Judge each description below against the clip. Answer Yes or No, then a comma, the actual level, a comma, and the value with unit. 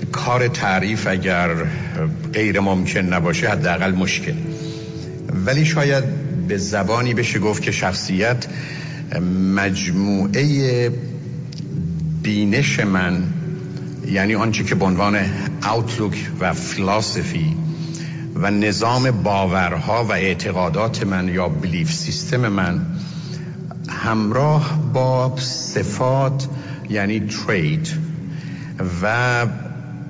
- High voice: No, low, 130 Hz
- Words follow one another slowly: Yes, slow, 85 wpm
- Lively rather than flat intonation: Yes, wide, 7.6 semitones